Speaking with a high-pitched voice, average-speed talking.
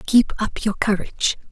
Yes: high, 210 Hz; average, 160 wpm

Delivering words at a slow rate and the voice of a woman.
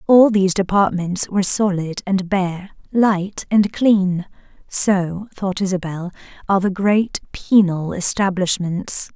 Yes: slow, 120 wpm; female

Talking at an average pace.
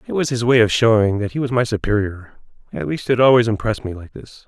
No: fast, 240 wpm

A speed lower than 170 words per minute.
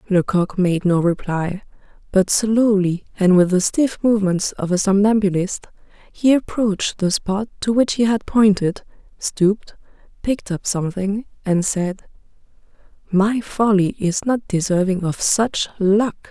Yes: slow, 135 wpm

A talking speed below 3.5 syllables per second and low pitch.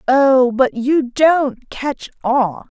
No: 2.5 syllables/s; very high, 265 Hz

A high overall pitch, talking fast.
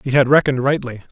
No: low, 135 Hz; fast, 215 wpm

